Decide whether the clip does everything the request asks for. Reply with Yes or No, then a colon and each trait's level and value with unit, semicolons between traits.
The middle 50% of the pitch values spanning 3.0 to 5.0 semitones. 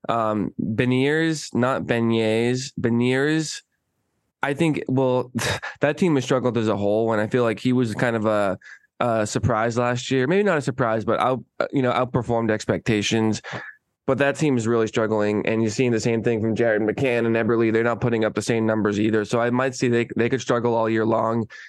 No: narrow, 2.6 semitones